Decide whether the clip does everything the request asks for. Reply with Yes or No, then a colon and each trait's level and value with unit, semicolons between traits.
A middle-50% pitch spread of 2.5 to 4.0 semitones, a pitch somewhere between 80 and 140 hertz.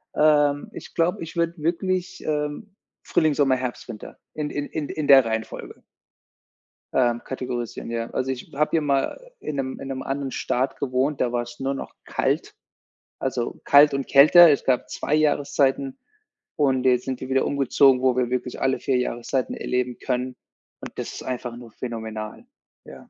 Yes: average, 2.8 semitones; low, 135 Hz